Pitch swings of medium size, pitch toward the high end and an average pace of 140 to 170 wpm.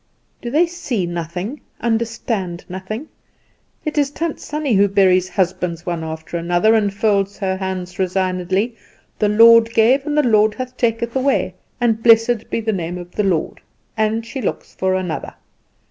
Yes: average, 4.1 semitones; high, 210 Hz; average, 160 wpm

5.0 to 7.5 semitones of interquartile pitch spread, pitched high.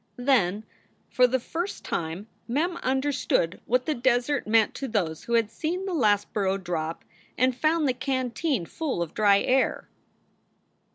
Yes: wide, 5.6 semitones; high, 245 Hz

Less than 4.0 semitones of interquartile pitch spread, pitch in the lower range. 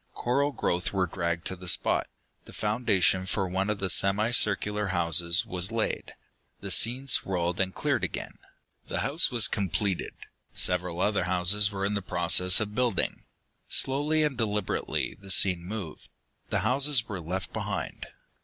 Yes: average, 3.6 semitones; low, 100 Hz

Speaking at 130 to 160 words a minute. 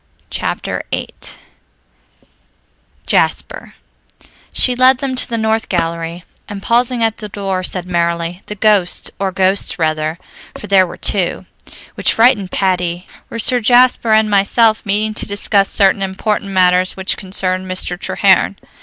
Yes: average, 140 wpm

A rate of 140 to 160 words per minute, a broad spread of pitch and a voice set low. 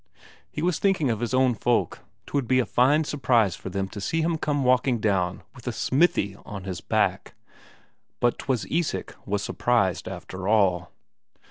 No: average, 170 wpm; wide, 5.9 semitones; low, 120 Hz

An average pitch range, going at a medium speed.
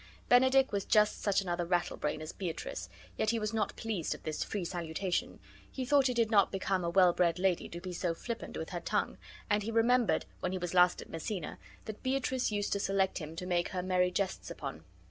No: average, 3.9 semitones; fast, 220 wpm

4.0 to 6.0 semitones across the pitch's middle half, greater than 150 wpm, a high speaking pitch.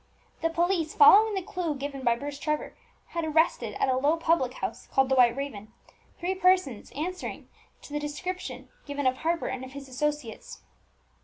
Yes: average, 4.3 semitones; average, 170 wpm; very high, 290 Hz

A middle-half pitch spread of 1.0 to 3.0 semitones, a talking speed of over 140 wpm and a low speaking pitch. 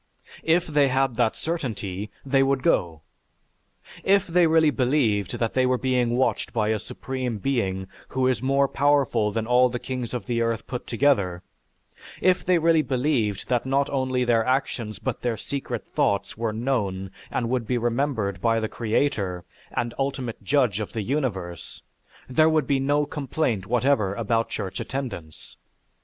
No: average, 4.0 semitones; average, 165 wpm; low, 125 Hz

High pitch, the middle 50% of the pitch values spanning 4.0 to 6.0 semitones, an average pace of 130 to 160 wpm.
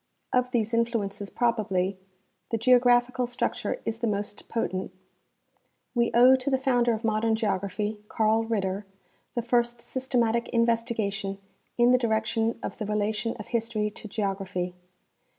No: high, 225 Hz; narrow, 2.4 semitones; average, 140 wpm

